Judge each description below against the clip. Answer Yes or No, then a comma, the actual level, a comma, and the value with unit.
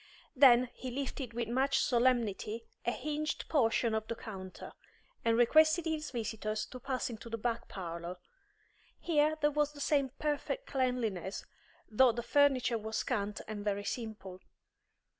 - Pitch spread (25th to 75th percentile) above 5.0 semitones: No, average, 4.3 semitones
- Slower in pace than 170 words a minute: Yes, average, 145 wpm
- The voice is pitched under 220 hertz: No, high, 240 Hz